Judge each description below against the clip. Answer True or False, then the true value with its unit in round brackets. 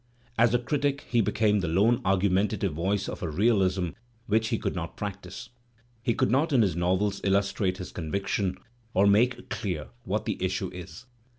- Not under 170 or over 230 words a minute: True (175 wpm)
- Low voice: True (100 Hz)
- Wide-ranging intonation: False (3.6 semitones)